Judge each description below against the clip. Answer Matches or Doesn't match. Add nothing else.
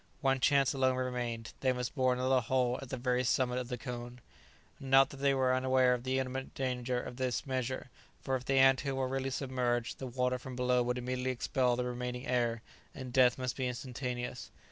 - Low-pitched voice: Matches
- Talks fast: Matches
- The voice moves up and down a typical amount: Doesn't match